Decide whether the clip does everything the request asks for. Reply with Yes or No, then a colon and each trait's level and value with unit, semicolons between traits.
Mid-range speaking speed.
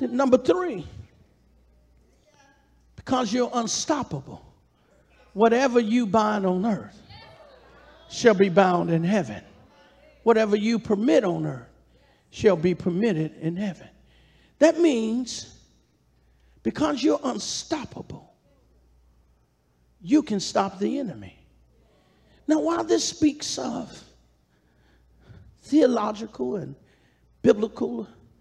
No: slow, 90 wpm